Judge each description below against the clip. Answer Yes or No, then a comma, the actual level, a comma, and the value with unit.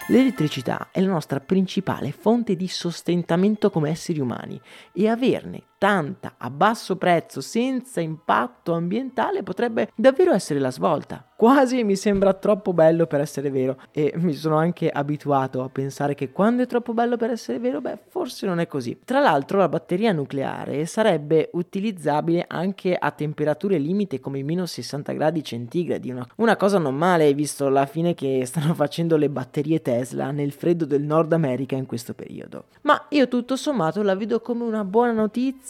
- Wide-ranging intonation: Yes, wide, 6.9 semitones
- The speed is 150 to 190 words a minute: Yes, fast, 170 wpm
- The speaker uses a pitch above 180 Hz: No, medium, 170 Hz